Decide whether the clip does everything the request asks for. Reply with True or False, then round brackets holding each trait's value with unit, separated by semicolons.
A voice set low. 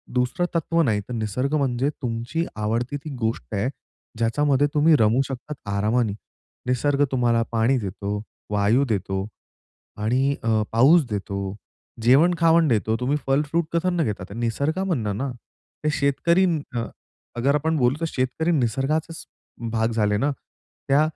True (125 Hz)